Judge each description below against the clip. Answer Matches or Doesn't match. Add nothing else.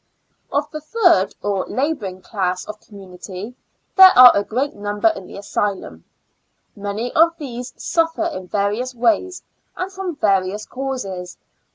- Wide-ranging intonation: Matches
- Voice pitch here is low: Doesn't match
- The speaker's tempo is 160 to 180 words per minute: Doesn't match